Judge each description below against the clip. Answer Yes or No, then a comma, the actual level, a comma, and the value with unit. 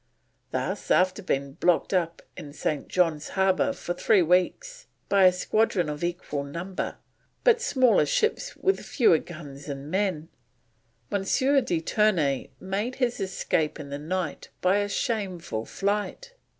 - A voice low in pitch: No, medium, 185 Hz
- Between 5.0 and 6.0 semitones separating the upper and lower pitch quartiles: Yes, average, 5.3 semitones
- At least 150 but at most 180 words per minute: No, average, 140 wpm